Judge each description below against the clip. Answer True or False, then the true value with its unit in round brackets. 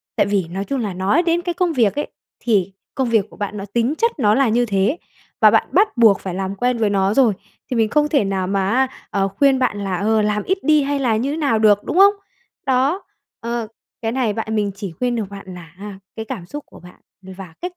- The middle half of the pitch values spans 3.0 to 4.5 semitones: False (5.2 semitones)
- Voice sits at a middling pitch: False (220 Hz)